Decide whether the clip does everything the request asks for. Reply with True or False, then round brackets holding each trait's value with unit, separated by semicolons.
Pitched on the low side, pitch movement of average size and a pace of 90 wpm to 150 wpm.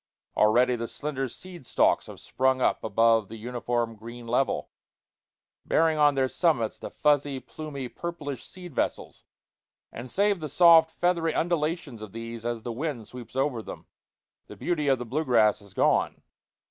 False (130 Hz; 5.0 semitones; 160 wpm)